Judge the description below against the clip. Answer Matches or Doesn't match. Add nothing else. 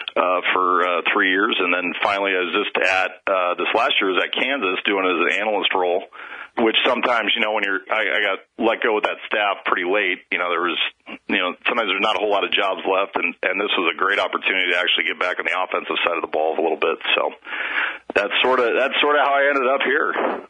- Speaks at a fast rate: Matches